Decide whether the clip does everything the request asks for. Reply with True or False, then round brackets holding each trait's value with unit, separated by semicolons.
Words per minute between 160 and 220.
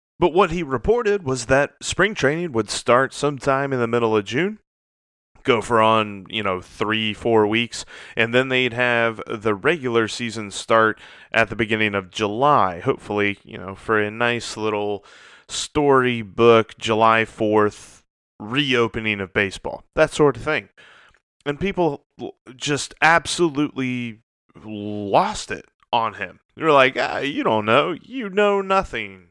False (145 wpm)